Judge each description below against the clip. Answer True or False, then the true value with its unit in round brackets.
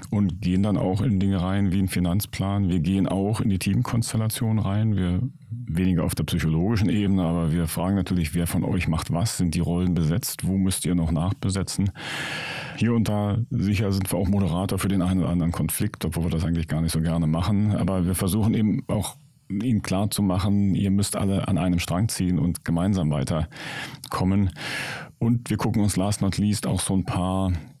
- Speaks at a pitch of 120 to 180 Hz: False (95 Hz)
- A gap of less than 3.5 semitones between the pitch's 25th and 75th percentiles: True (2.7 semitones)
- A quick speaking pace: True (205 wpm)